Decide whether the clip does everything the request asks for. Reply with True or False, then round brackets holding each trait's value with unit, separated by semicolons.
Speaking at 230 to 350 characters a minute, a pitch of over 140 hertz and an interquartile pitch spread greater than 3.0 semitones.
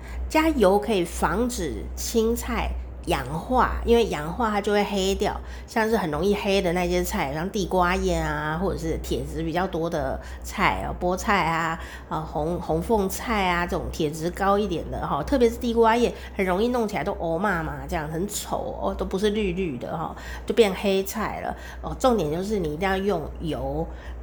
True (265 characters per minute; 190 Hz; 4.2 semitones)